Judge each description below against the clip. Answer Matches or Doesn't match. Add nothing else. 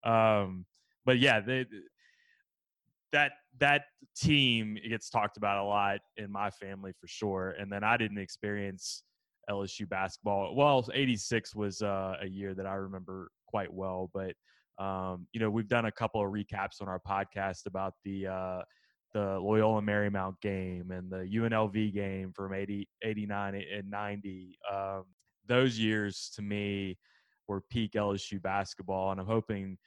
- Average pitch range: Doesn't match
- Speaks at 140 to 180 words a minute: Matches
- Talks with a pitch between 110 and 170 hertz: Doesn't match